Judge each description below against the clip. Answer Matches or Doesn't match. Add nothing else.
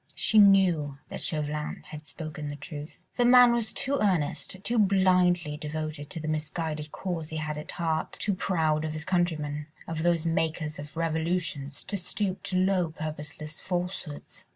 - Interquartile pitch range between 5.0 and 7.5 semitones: Doesn't match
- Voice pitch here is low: Doesn't match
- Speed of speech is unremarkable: Matches